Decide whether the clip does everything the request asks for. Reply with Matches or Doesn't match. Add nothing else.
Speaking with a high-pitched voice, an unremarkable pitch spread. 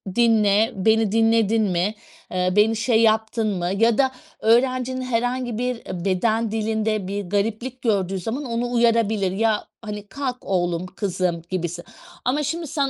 Matches